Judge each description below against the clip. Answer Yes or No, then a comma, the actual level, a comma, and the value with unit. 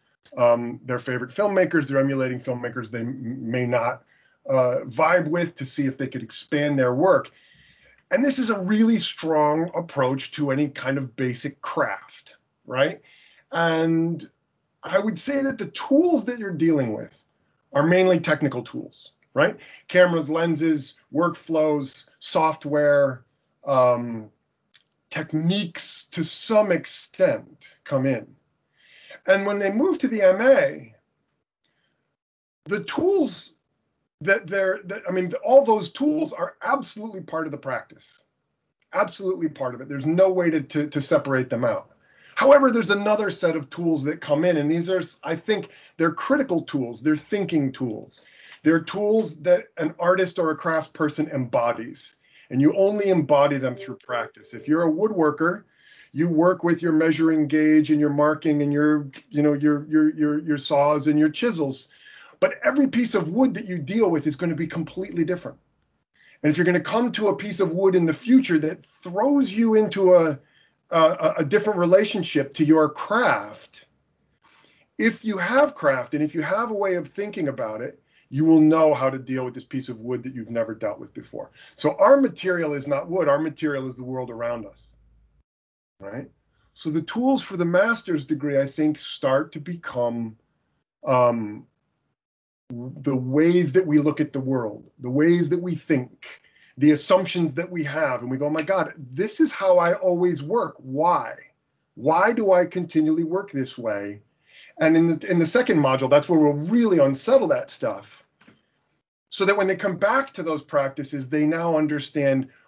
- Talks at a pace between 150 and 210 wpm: Yes, average, 170 wpm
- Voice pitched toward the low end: No, medium, 160 Hz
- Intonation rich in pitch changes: No, average, 5.0 semitones